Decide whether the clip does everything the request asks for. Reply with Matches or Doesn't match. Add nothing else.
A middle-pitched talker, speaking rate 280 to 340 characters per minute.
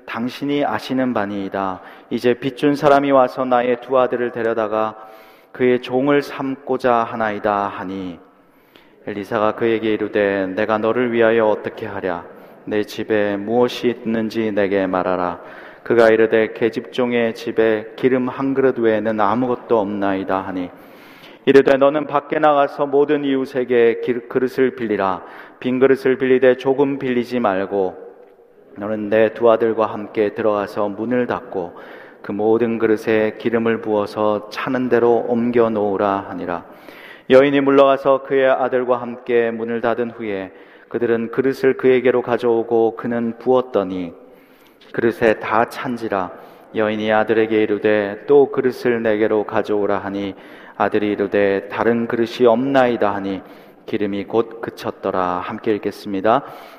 Doesn't match